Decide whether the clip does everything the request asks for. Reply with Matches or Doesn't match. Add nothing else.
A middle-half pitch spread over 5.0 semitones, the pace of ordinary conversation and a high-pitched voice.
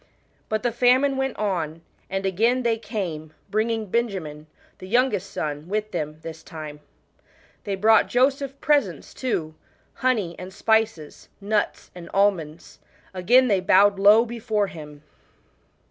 Doesn't match